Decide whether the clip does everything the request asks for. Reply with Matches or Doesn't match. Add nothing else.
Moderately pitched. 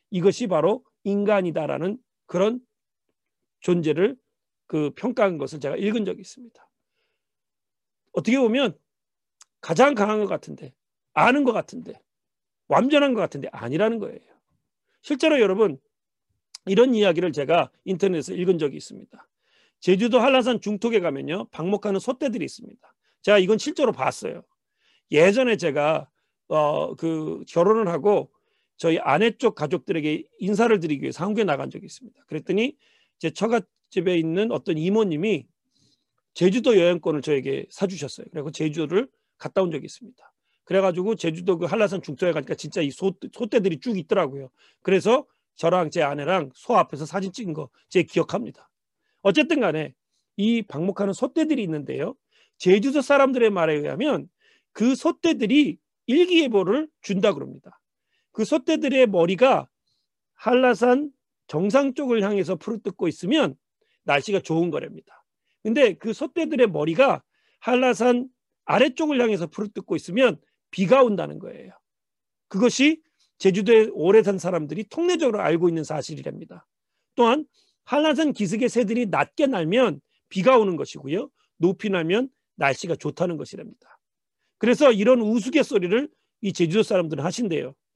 Doesn't match